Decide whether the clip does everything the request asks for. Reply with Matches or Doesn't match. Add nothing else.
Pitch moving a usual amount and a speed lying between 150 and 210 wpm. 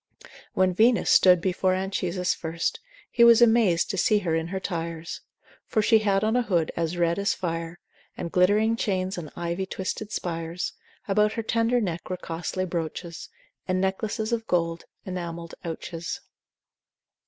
Matches